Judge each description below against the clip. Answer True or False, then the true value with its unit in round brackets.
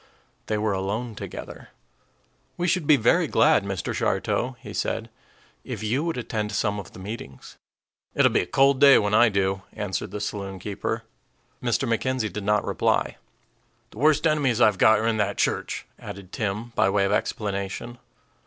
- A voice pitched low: True (110 Hz)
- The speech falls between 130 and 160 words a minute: False (170 wpm)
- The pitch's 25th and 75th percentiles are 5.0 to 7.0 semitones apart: False (4.0 semitones)